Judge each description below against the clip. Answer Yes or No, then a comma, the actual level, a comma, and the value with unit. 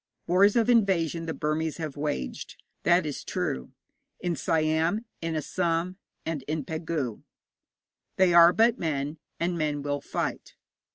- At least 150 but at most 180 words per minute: No, slow, 135 wpm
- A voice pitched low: No, medium, 165 Hz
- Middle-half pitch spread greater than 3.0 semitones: No, average, 2.7 semitones